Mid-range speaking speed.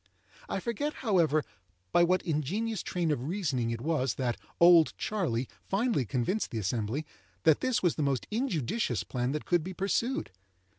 Yes: average, 160 wpm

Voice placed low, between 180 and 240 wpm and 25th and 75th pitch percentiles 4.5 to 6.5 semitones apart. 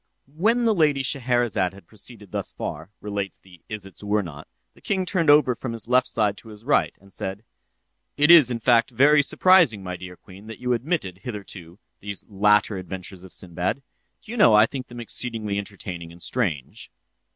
Yes: low, 110 Hz; average, 185 wpm; average, 5.2 semitones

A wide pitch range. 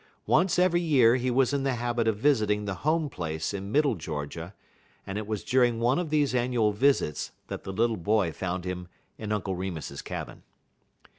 Yes: wide, 5.8 semitones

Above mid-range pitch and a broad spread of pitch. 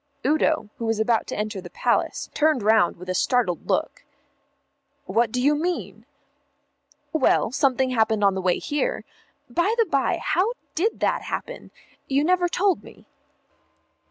Yes: very high, 255 Hz; wide, 6.7 semitones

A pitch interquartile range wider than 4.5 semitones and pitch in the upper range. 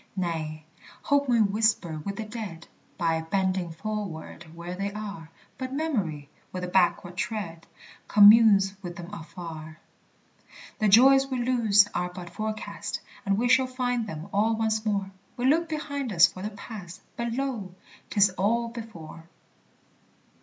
Yes: average, 4.9 semitones; high, 200 Hz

